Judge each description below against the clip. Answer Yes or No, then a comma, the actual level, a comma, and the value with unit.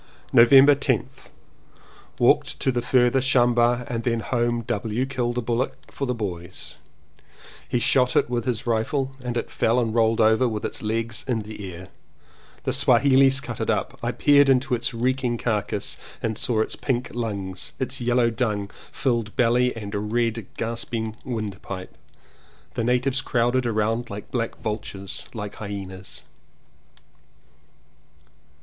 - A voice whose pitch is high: No, low, 120 Hz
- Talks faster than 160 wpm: No, average, 145 wpm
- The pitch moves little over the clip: Yes, narrow, 2.3 semitones